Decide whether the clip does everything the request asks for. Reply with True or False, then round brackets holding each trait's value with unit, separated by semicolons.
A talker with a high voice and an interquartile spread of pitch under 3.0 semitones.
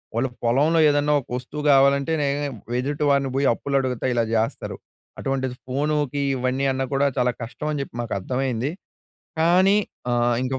False (135 Hz; 2.6 semitones)